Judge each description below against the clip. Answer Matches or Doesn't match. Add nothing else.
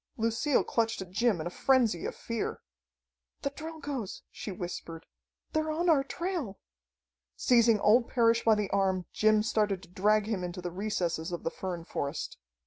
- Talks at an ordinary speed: Matches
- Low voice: Doesn't match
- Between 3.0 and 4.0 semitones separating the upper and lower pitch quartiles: Doesn't match